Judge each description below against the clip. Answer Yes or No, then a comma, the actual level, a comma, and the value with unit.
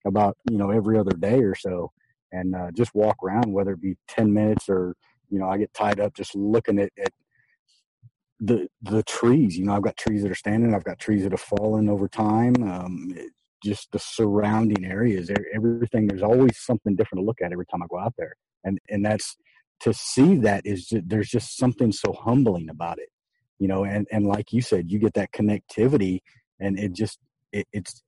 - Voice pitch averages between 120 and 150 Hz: No, low, 105 Hz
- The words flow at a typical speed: No, fast, 210 wpm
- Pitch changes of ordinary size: No, narrow, 2.1 semitones